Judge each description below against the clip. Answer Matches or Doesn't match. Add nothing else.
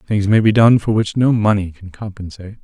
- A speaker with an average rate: Doesn't match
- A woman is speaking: Doesn't match